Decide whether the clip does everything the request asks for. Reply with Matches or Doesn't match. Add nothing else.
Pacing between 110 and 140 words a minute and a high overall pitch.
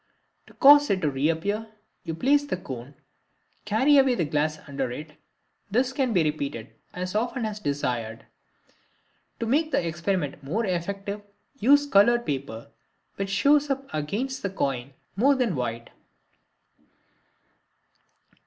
Matches